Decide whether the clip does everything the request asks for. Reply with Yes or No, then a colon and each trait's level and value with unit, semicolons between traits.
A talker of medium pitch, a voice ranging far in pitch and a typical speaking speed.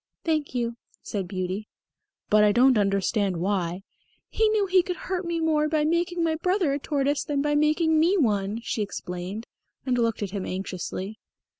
No: very high, 255 Hz; wide, 8.1 semitones; average, 180 wpm